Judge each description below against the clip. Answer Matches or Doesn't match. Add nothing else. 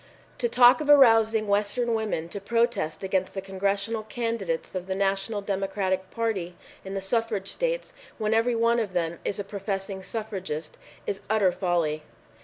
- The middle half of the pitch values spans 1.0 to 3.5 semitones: Matches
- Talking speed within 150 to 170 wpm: Matches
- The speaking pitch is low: Doesn't match